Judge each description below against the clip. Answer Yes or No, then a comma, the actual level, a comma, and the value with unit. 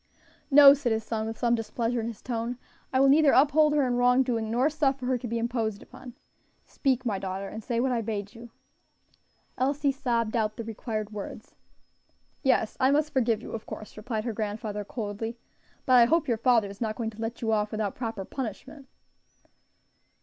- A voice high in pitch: Yes, high, 235 Hz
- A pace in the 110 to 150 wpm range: No, average, 195 wpm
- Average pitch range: Yes, average, 3.1 semitones